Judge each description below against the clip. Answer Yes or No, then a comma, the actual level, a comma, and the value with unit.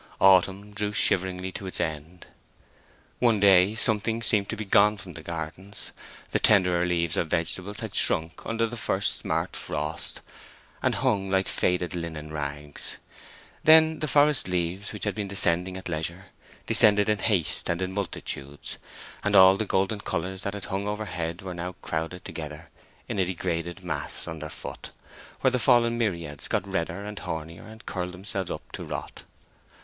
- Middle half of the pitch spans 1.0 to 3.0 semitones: No, average, 3.4 semitones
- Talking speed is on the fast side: No, average, 165 wpm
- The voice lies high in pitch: No, very low, 95 Hz